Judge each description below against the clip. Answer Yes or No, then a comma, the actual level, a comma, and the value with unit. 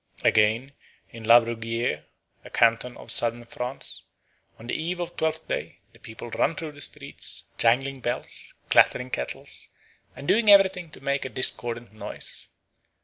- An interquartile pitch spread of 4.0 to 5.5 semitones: Yes, average, 4.3 semitones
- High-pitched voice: No, low, 125 Hz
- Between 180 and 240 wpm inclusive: No, average, 145 wpm